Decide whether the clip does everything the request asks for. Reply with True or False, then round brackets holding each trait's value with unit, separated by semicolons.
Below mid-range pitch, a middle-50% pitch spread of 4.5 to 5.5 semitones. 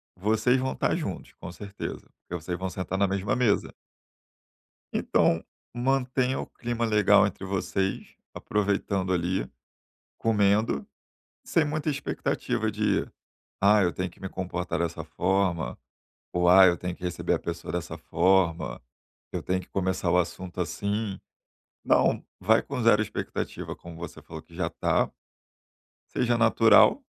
False (95 Hz; 3.7 semitones)